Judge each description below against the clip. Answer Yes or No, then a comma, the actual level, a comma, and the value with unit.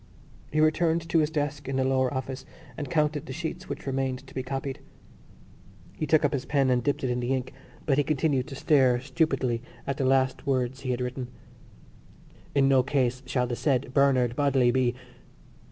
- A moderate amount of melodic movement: No, narrow, 2.2 semitones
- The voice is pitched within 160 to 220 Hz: No, low, 135 Hz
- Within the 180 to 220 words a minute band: Yes, average, 195 wpm